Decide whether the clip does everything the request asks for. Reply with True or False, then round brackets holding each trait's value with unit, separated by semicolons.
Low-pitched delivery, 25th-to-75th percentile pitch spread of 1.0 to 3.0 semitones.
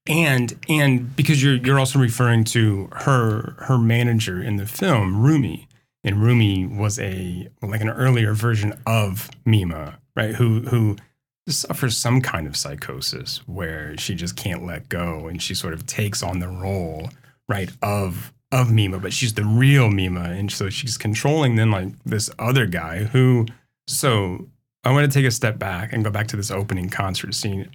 False (110 Hz; 4.8 semitones)